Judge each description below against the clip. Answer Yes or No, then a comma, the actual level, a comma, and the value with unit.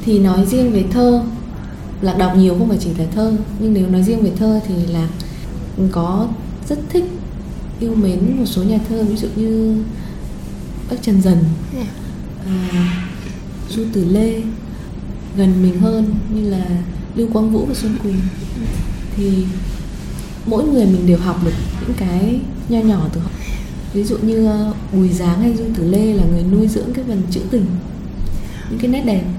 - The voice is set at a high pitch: Yes, high, 200 Hz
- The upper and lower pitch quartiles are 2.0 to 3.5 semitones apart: Yes, average, 3.2 semitones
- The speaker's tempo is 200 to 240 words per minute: No, average, 175 wpm